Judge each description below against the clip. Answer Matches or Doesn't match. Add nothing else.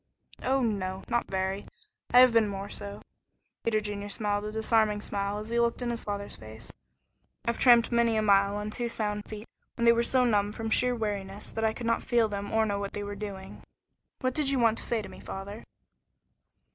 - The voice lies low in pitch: Doesn't match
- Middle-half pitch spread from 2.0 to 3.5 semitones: Matches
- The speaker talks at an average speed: Doesn't match